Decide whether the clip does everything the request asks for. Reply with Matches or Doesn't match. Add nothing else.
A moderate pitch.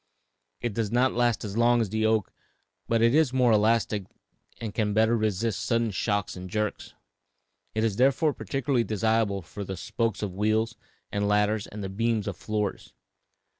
Doesn't match